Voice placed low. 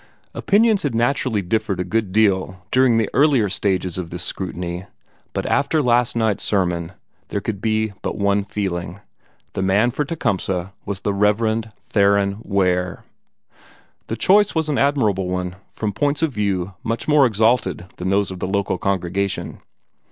Yes: low, 100 Hz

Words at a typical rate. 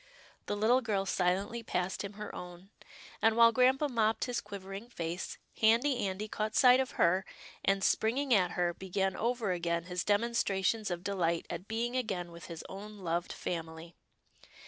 Yes: average, 170 wpm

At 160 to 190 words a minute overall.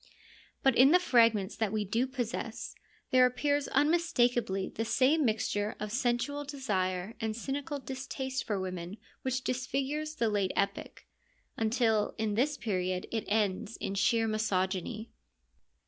No: slow, 135 wpm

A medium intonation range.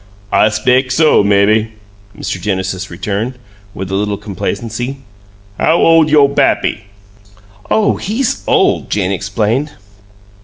No: wide, 5.8 semitones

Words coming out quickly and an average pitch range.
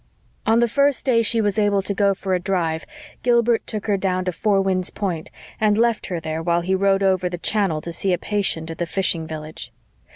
Yes: fast, 225 wpm; average, 3.5 semitones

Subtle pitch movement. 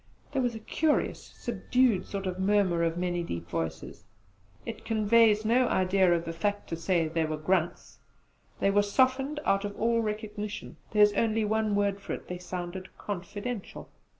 No: average, 3.7 semitones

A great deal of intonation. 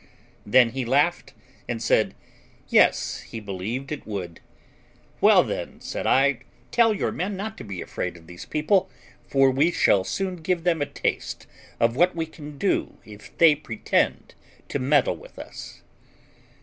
Yes: wide, 6.8 semitones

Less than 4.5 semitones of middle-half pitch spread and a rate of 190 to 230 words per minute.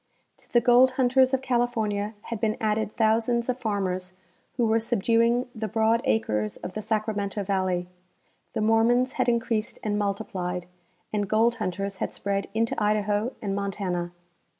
No: average, 2.8 semitones; average, 150 wpm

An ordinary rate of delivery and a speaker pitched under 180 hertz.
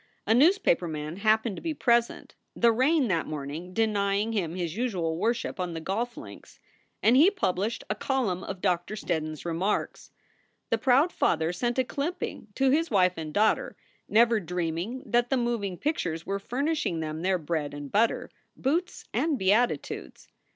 No: average, 165 wpm; high, 205 Hz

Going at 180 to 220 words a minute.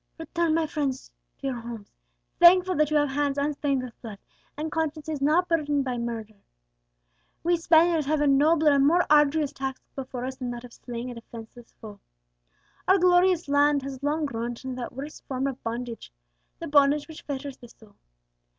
Yes: average, 185 wpm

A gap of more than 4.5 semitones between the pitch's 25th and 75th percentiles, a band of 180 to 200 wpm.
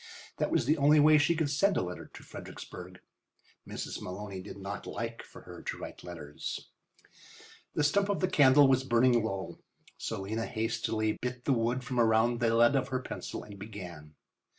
Yes: average, 5.2 semitones; average, 185 wpm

